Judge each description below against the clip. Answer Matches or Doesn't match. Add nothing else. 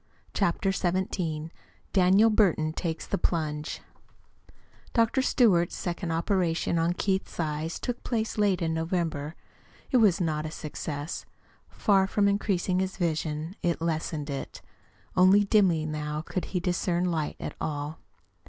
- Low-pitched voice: Doesn't match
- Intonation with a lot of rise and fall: Doesn't match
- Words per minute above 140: Doesn't match